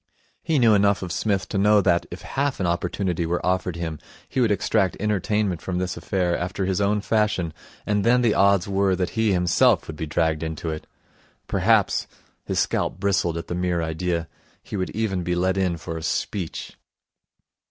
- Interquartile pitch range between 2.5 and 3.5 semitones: Yes, average, 2.9 semitones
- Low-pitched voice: Yes, very low, 95 Hz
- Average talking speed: Yes, average, 190 wpm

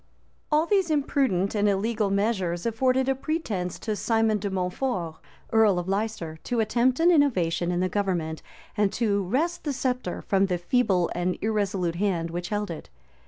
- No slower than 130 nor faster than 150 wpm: No, average, 170 wpm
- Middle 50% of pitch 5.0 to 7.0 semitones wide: Yes, wide, 5.6 semitones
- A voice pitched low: No, high, 205 Hz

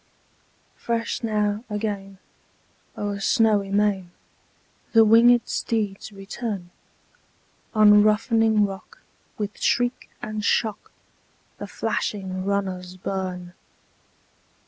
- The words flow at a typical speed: No, slow, 85 wpm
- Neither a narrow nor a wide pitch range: No, narrow, 2.1 semitones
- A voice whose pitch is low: No, high, 210 Hz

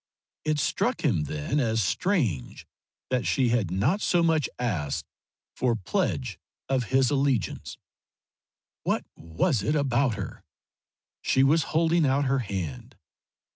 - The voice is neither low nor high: No, low, 130 Hz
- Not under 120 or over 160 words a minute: Yes, slow, 135 wpm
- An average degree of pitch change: No, wide, 6.7 semitones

